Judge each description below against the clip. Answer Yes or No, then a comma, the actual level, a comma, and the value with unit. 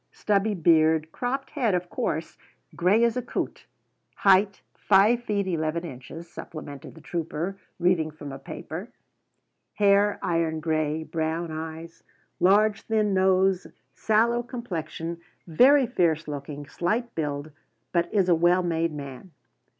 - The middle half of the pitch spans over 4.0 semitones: Yes, average, 4.4 semitones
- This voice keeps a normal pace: No, slow, 130 wpm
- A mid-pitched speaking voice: Yes, medium, 175 Hz